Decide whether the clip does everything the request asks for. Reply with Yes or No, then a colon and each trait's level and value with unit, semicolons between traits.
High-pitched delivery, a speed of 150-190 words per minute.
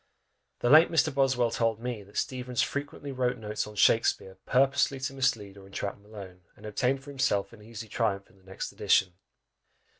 No: low, 115 Hz; average, 180 wpm